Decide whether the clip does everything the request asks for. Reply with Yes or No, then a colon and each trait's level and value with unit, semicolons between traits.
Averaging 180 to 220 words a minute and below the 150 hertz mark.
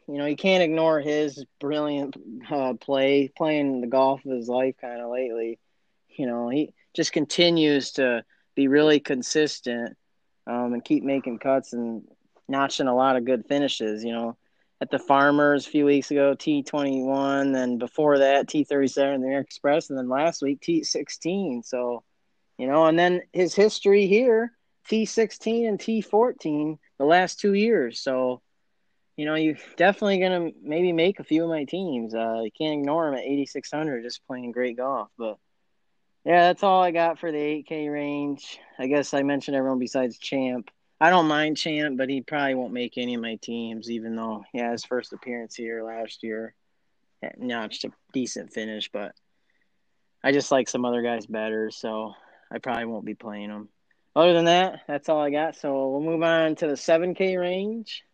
Yes: average, 185 wpm; medium, 140 Hz